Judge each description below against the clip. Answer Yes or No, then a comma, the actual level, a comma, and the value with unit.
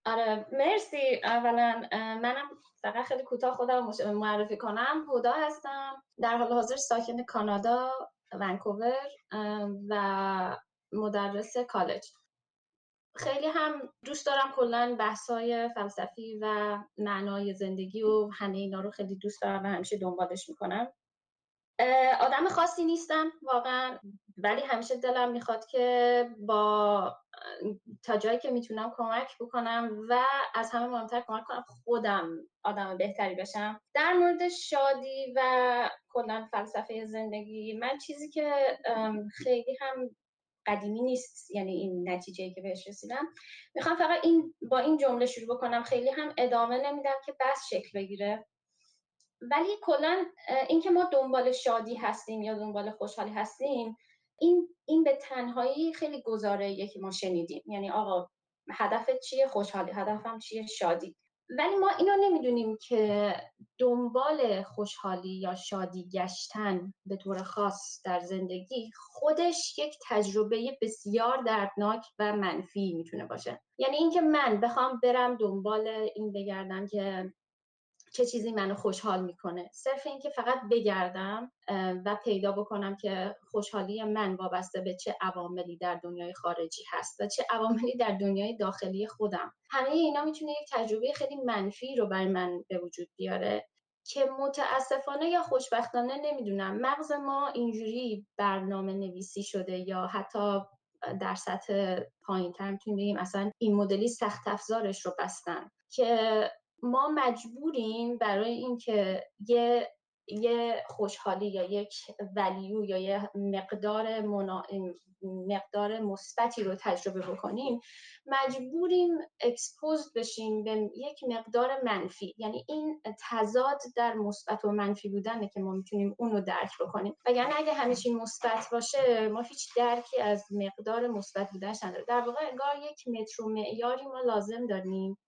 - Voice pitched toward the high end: Yes, high, 225 Hz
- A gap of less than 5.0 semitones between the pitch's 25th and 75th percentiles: Yes, average, 4.3 semitones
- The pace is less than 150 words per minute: Yes, average, 135 wpm